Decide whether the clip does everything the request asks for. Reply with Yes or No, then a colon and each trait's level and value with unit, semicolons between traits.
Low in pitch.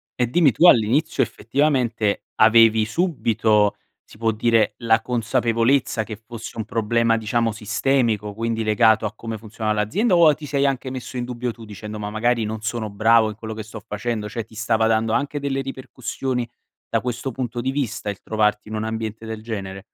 Yes: low, 115 Hz